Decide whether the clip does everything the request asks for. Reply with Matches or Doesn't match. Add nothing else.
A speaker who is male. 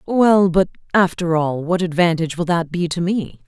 Doesn't match